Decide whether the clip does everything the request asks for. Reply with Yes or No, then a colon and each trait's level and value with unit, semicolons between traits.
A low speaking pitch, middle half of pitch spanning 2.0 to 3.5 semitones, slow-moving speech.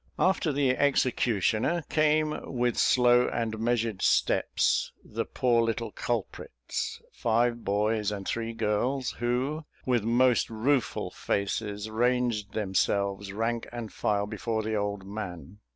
Yes: low, 115 Hz; average, 3.0 semitones; slow, 120 wpm